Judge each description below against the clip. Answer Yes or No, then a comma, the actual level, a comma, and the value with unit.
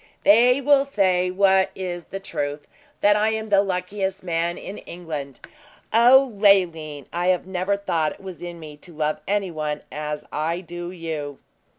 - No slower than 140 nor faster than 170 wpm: Yes, average, 165 wpm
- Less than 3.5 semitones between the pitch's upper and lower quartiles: No, average, 3.8 semitones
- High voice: No, medium, 180 Hz